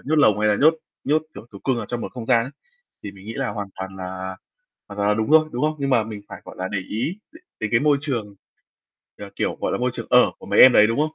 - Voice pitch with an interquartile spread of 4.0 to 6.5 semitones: Yes, average, 4.9 semitones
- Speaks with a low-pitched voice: Yes, low, 115 Hz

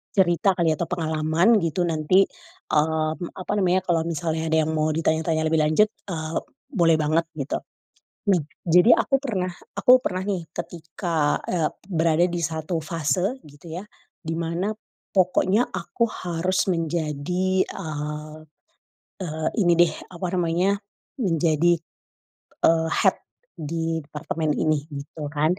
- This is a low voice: No, medium, 165 Hz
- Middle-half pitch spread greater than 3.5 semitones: No, narrow, 2.5 semitones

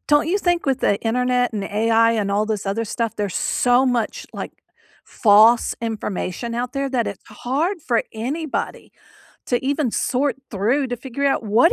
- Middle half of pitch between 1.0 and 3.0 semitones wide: No, average, 3.7 semitones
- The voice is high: Yes, high, 240 Hz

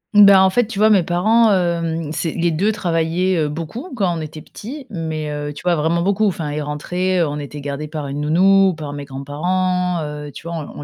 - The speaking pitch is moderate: Yes, medium, 170 Hz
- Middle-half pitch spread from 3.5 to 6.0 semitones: Yes, average, 4.0 semitones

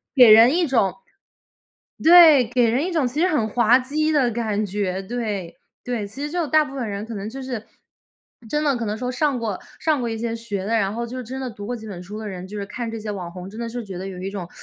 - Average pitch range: Yes, average, 4.2 semitones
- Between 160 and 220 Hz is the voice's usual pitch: No, high, 230 Hz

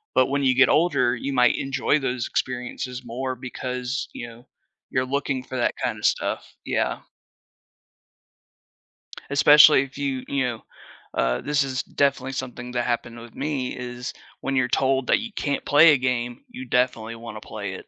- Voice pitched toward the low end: Yes, low, 130 Hz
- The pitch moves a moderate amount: No, narrow, 2.1 semitones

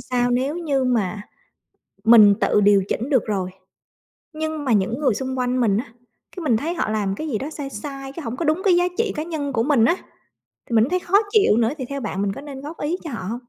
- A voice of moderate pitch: No, very high, 260 Hz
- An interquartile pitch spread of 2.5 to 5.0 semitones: No, wide, 5.4 semitones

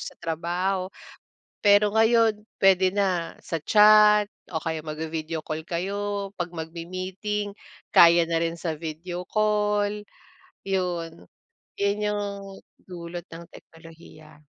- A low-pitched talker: No, medium, 180 Hz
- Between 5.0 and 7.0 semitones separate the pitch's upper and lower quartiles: No, average, 3.6 semitones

